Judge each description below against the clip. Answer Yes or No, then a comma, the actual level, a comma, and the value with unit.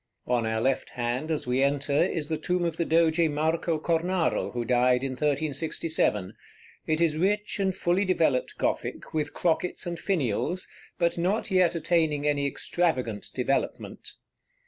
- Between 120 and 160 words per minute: Yes, average, 150 wpm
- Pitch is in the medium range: Yes, medium, 155 Hz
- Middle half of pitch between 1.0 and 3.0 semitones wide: No, average, 4.1 semitones